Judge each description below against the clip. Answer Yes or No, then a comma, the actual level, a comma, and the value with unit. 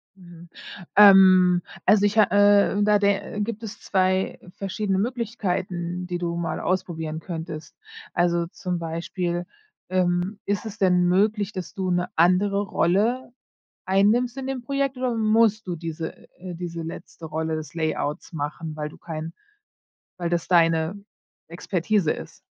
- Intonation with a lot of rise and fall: No, average, 3.3 semitones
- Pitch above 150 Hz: Yes, medium, 185 Hz